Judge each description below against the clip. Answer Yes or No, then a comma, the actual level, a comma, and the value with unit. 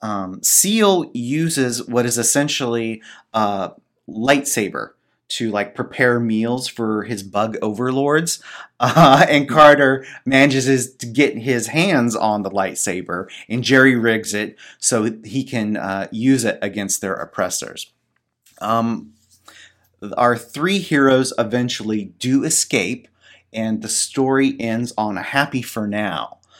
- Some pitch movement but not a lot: Yes, average, 3.6 semitones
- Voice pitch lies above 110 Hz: Yes, low, 120 Hz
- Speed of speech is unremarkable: No, slow, 130 wpm